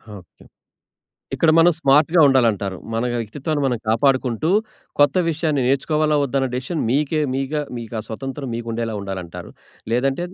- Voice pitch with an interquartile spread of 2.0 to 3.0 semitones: No, average, 4.5 semitones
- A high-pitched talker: No, low, 135 Hz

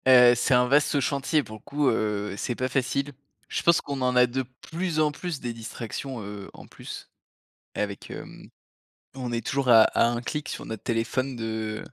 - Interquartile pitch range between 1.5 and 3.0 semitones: No, average, 3.6 semitones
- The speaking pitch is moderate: No, low, 125 Hz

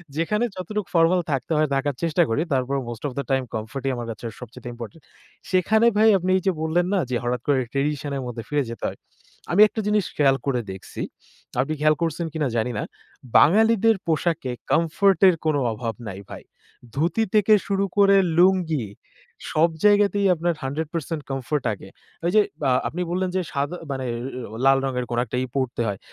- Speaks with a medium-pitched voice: Yes, medium, 155 Hz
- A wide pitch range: Yes, wide, 5.7 semitones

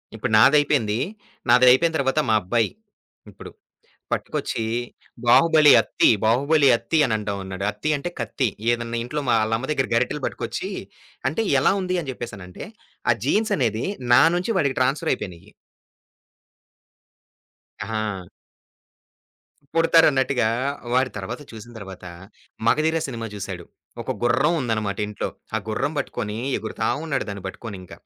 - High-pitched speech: No, low, 120 Hz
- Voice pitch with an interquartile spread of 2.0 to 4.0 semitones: No, average, 5.1 semitones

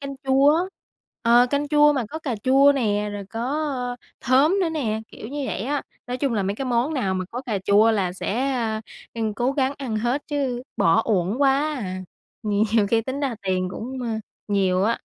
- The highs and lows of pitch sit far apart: No, average, 4.8 semitones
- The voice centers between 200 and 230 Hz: No, high, 245 Hz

